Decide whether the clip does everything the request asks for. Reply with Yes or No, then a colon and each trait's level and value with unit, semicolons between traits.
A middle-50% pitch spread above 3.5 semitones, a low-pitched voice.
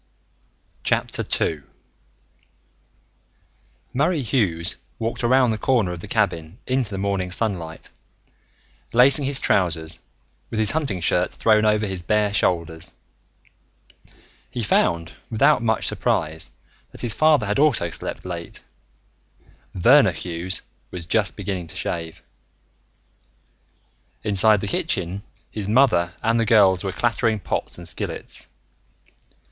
Yes: average, 4.8 semitones; low, 100 Hz